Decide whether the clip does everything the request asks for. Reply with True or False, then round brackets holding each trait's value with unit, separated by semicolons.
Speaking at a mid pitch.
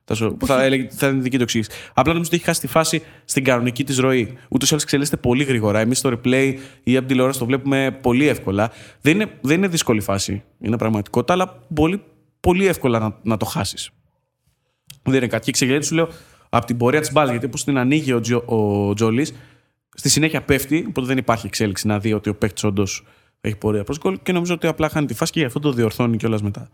False (130 Hz)